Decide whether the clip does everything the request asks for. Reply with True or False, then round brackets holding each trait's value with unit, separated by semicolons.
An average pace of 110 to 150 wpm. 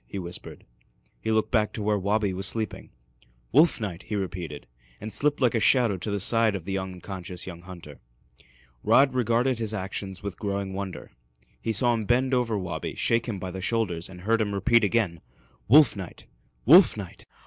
False (185 wpm)